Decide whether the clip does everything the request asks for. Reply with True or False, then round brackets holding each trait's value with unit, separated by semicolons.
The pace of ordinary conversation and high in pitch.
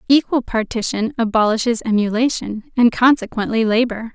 False (100 wpm; 230 Hz)